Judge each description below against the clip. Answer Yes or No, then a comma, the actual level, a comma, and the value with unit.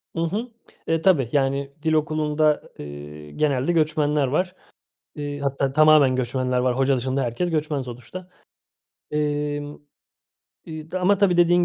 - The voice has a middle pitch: Yes, medium, 145 Hz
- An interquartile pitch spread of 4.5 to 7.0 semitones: No, average, 3.2 semitones